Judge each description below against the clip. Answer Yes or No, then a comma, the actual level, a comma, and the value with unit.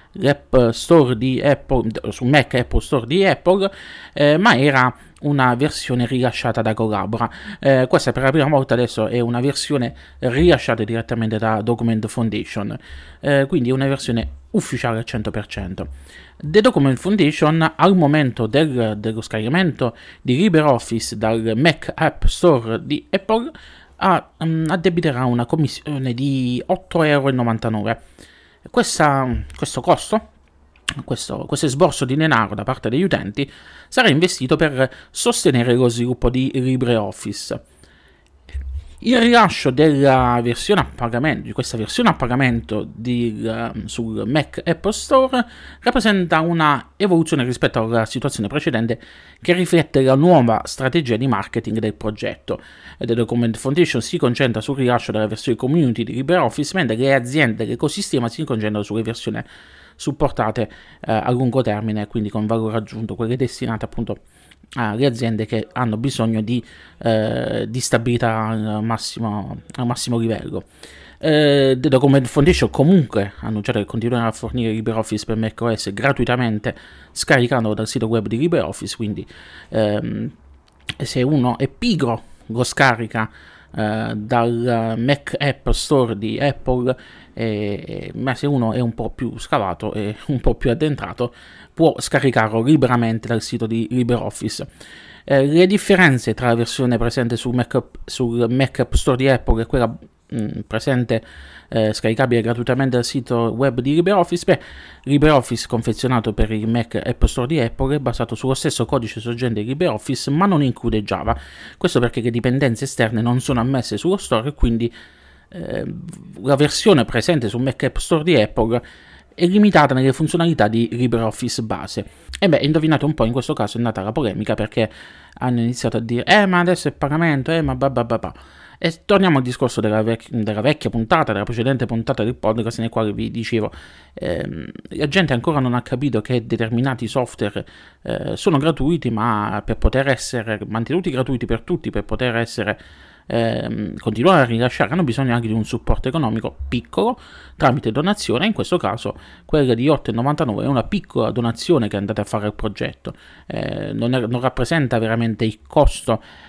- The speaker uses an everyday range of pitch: Yes, average, 4.2 semitones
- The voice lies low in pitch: Yes, low, 120 Hz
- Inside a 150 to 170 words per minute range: Yes, average, 155 wpm